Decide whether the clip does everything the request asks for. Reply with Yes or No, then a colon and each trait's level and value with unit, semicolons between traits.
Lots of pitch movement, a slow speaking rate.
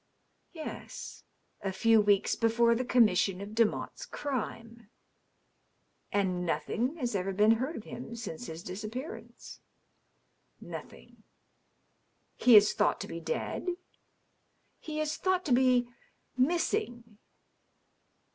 No: average, 3.8 semitones; slow, 130 wpm